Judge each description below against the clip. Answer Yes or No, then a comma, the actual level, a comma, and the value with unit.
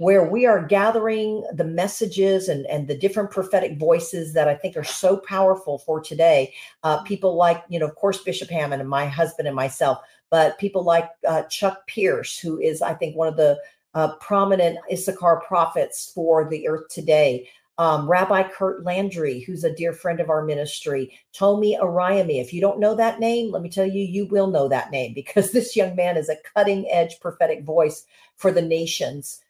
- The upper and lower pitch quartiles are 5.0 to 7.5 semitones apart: No, average, 3.7 semitones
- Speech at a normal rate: Yes, average, 195 wpm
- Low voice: No, medium, 175 Hz